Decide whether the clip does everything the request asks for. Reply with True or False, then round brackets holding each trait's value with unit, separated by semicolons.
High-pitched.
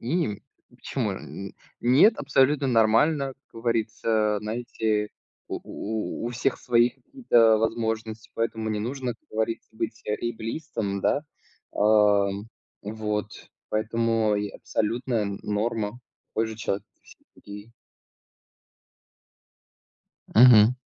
False (115 Hz)